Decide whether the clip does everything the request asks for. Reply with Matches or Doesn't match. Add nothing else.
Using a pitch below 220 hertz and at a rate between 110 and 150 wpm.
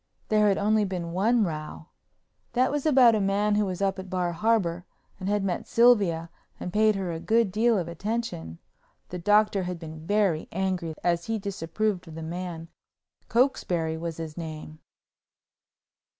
Doesn't match